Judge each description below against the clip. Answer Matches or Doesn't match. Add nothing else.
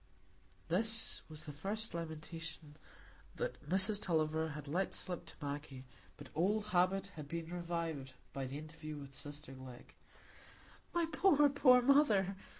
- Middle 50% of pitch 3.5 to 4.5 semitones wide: Doesn't match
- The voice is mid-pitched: Matches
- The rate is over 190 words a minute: Doesn't match